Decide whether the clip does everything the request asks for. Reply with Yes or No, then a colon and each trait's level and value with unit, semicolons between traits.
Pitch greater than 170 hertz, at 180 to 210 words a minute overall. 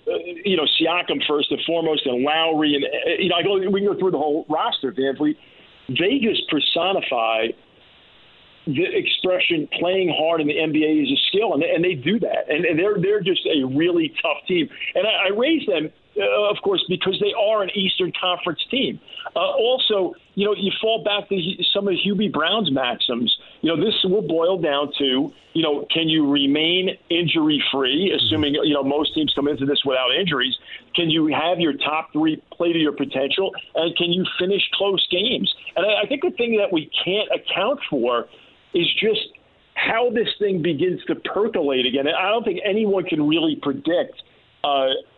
Yes: medium, 185 Hz; average, 195 wpm